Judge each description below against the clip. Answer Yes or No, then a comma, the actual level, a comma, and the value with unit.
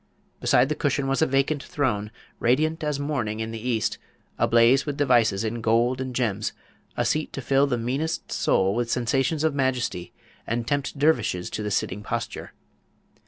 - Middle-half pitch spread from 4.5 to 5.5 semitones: No, average, 3.8 semitones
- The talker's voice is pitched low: Yes, low, 125 Hz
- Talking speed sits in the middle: Yes, average, 170 wpm